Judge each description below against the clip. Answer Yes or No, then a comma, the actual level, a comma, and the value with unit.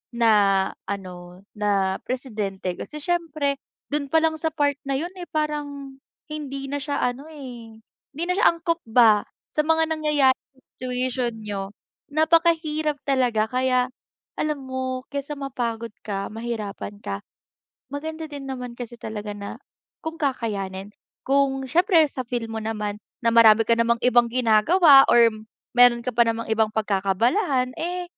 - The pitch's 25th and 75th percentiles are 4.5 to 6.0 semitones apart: Yes, average, 5.0 semitones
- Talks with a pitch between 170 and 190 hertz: No, very high, 255 Hz